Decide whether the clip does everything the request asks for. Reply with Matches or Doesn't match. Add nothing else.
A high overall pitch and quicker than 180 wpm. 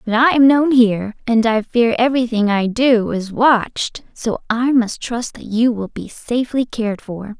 Matches